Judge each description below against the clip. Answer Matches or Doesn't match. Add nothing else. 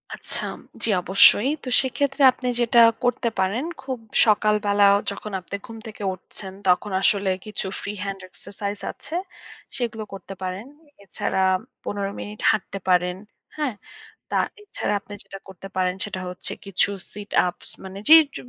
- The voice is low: Doesn't match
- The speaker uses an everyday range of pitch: Matches